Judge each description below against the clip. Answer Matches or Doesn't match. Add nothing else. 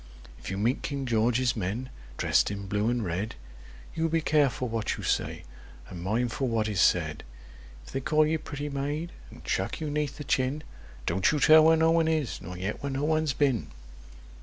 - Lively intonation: Matches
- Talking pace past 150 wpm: Matches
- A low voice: Matches